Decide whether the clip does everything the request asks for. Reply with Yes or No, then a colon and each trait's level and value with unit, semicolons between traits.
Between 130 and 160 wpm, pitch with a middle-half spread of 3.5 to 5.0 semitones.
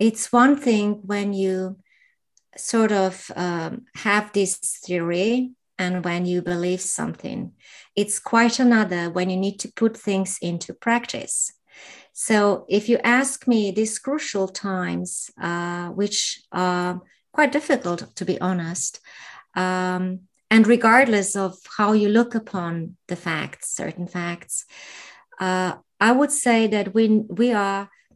Yes: slow, 135 wpm; average, 3.8 semitones